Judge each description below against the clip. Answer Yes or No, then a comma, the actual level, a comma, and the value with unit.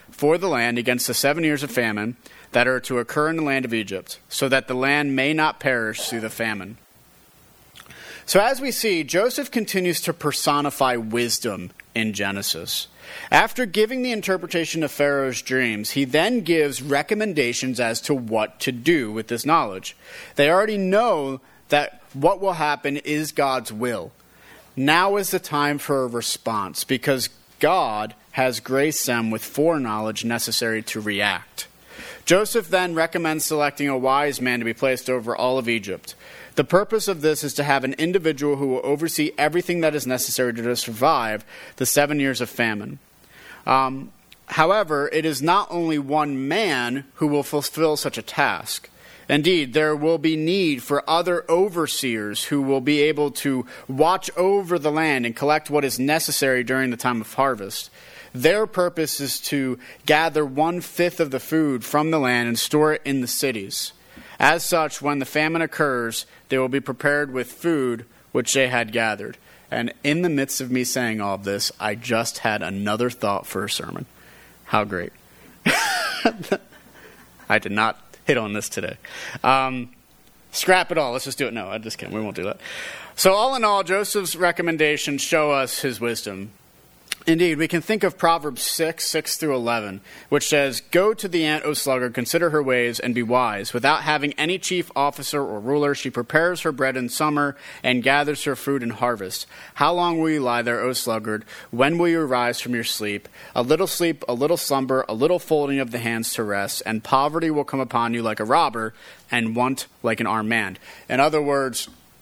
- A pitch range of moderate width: Yes, average, 4.5 semitones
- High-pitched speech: No, medium, 140 Hz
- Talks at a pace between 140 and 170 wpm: No, average, 180 wpm